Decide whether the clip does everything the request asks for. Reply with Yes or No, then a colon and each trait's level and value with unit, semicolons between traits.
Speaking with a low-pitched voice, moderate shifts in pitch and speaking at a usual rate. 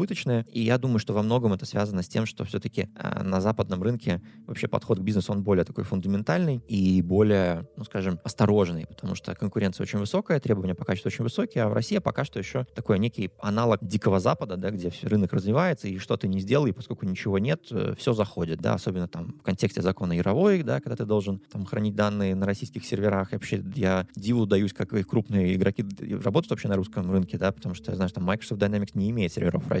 No: low, 105 Hz; average, 3.2 semitones; fast, 215 wpm